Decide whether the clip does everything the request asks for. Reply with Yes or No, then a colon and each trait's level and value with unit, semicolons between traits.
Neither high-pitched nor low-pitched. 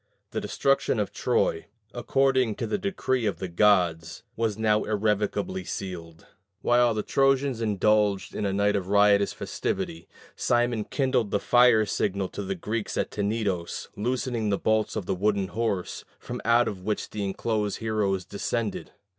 No: low, 105 Hz